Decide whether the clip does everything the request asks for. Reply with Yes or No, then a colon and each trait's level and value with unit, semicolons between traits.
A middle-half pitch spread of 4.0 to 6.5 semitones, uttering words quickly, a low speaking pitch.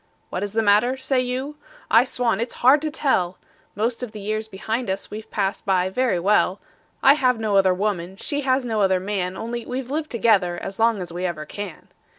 No: average, 4.6 semitones; fast, 210 wpm; high, 215 Hz